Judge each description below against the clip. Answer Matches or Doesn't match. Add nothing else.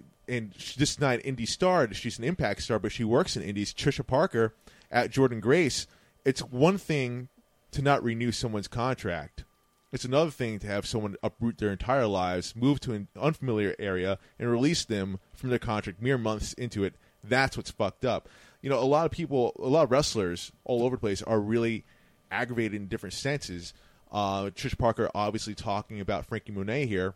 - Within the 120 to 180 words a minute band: Doesn't match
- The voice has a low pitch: Matches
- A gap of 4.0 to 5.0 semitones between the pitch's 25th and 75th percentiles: Matches